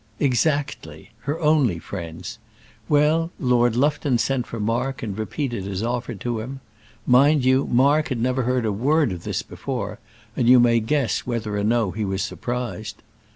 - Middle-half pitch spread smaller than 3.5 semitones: No, average, 3.8 semitones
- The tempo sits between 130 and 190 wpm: Yes, average, 165 wpm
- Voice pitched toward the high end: No, low, 125 Hz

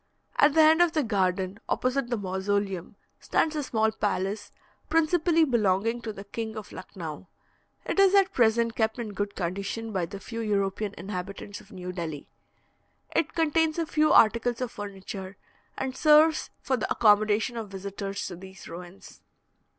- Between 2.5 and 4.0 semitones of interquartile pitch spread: No, average, 4.9 semitones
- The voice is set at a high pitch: Yes, high, 215 Hz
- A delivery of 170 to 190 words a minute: No, average, 160 wpm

